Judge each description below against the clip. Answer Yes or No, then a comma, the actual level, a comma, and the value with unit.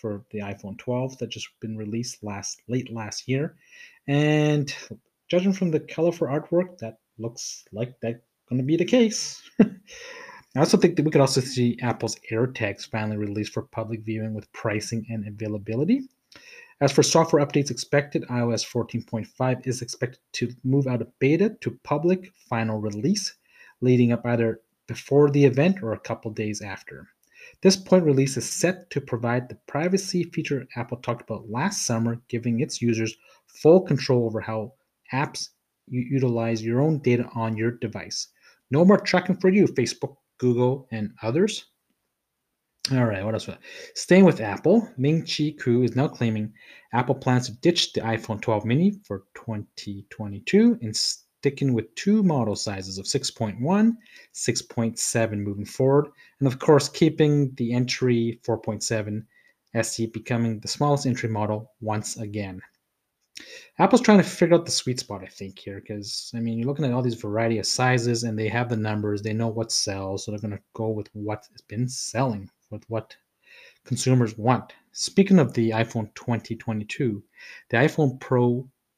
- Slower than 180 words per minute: Yes, average, 165 wpm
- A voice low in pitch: Yes, low, 120 Hz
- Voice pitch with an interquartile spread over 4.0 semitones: Yes, average, 4.6 semitones